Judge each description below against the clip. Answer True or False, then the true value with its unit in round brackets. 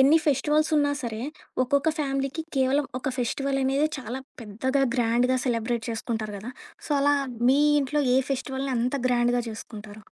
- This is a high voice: True (260 Hz)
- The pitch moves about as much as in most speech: True (3.0 semitones)